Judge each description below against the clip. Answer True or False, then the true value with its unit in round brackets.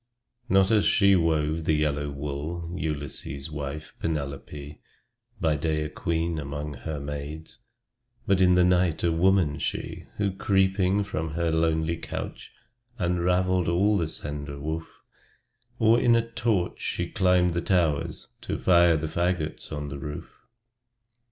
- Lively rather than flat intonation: False (3.5 semitones)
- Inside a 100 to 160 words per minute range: True (140 wpm)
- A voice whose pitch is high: False (80 Hz)